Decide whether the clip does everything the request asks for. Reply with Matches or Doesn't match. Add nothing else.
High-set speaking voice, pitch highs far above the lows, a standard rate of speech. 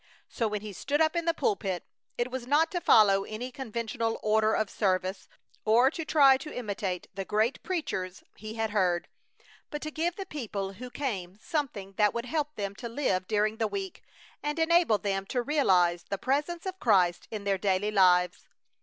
Matches